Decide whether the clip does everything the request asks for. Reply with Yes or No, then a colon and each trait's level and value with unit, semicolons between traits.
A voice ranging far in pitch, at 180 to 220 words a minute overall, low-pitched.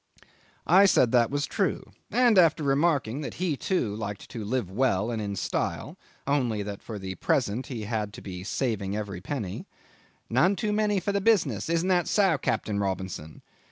Yes: wide, 8.6 semitones; average, 185 wpm; low, 120 Hz